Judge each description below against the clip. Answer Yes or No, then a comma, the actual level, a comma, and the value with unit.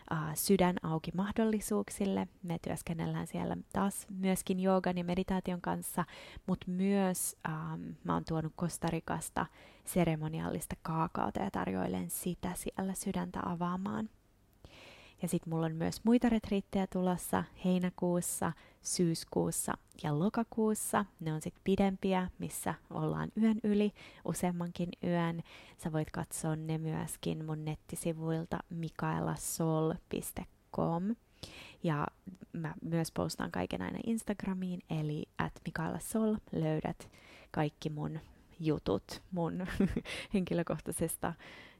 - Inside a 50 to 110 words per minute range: Yes, average, 105 wpm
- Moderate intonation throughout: Yes, average, 3.4 semitones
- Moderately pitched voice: Yes, medium, 175 Hz